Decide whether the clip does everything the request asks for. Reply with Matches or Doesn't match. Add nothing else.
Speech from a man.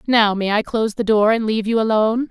Doesn't match